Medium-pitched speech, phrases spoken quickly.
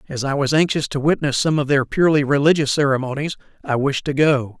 Yes: medium, 145 Hz; fast, 210 wpm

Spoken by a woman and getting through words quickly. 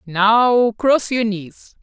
No: female; slow, 130 wpm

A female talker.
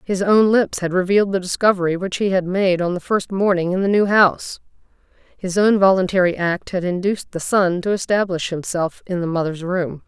Yes: female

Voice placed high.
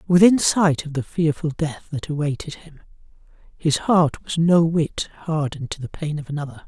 No: medium, 155 Hz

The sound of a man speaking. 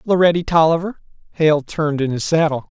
Yes: male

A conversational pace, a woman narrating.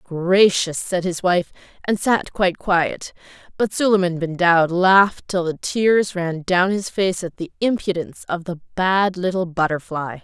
Yes: average, 165 wpm; female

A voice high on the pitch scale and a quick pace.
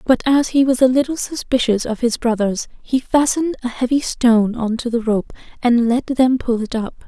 Yes: high, 245 Hz; fast, 210 wpm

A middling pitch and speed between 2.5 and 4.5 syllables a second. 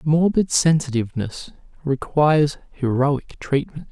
Yes: medium, 145 Hz; 4.2 syllables/s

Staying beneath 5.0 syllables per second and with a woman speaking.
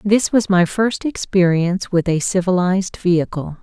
Yes: 4.8 syllables/s; female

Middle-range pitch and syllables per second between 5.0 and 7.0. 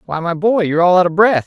No: medium, 180 Hz; 7.5 syllables/s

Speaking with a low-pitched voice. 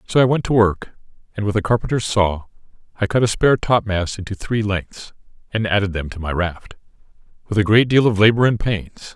Yes: low, 105 Hz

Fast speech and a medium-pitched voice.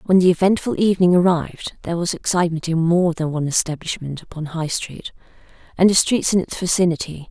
No: average, 180 wpm; medium, 170 Hz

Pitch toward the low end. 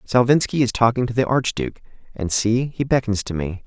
Yes: low, 120 Hz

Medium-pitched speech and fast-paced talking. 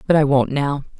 Yes: medium, 145 Hz; fast, 240 wpm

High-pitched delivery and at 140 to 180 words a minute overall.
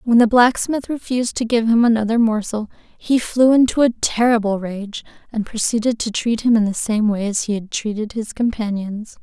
No: high, 225 Hz; average, 195 wpm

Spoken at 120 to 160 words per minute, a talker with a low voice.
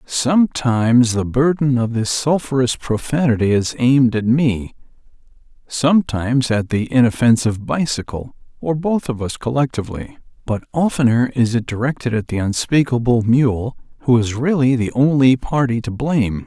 Yes: average, 140 wpm; low, 125 Hz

